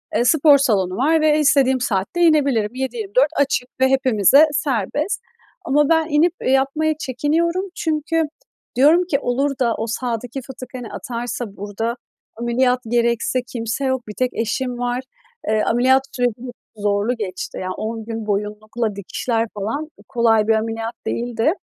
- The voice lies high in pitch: Yes, high, 245 Hz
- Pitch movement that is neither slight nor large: Yes, average, 3.8 semitones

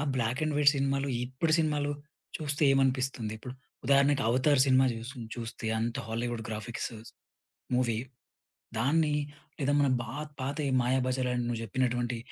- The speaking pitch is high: No, low, 130 Hz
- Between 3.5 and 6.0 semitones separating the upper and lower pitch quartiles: No, average, 2.8 semitones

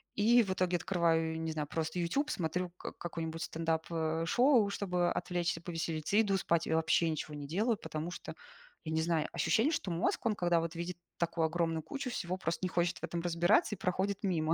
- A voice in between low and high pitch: Yes, medium, 170 Hz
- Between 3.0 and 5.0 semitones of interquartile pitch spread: No, narrow, 2.6 semitones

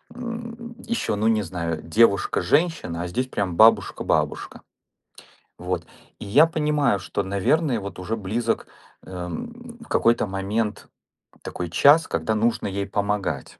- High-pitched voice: No, low, 110 Hz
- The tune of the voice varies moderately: No, wide, 8.0 semitones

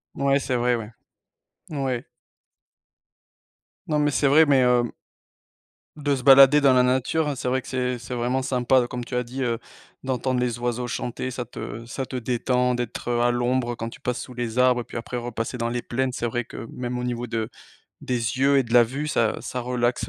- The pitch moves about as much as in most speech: No, narrow, 1.5 semitones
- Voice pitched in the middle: No, low, 125 Hz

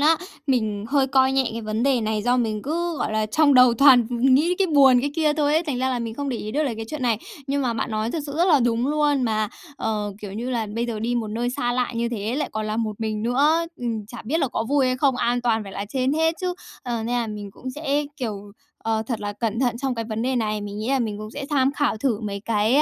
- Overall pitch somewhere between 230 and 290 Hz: Yes, high, 245 Hz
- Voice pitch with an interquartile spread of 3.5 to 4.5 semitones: Yes, average, 4.0 semitones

